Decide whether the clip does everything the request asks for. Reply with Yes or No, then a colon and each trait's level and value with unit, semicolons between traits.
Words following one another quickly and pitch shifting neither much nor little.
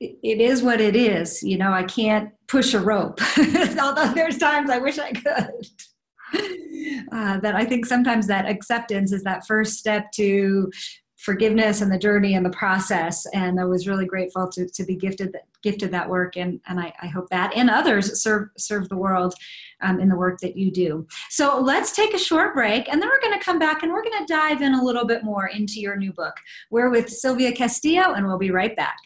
No: fast, 215 wpm; wide, 6.2 semitones